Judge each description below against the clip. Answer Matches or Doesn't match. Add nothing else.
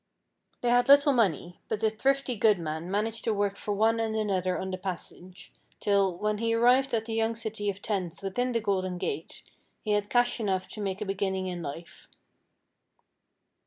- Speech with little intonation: Doesn't match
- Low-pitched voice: Doesn't match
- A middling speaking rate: Matches